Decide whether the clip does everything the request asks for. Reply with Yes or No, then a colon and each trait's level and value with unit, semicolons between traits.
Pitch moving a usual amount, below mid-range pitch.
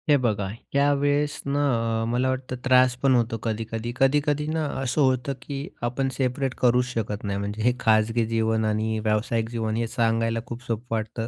Yes: average, 3.0 semitones; low, 120 Hz